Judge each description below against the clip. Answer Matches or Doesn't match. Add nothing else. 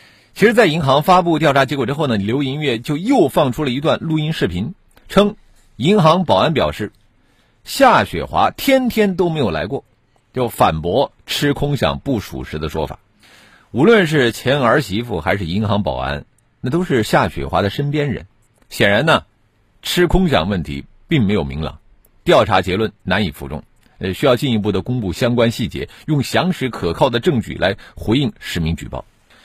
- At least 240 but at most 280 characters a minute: Matches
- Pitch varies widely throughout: Matches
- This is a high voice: Doesn't match